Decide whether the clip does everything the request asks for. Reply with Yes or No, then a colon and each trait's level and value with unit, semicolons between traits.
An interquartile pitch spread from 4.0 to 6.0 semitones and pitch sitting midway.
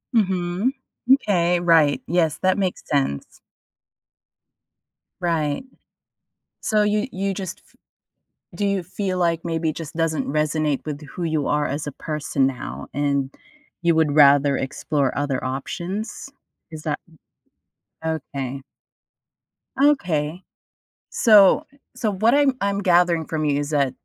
Yes: average, 4.4 semitones; medium, 160 Hz